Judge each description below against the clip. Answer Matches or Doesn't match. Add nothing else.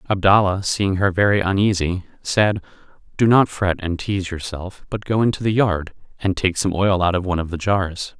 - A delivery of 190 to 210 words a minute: Matches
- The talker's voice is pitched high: Doesn't match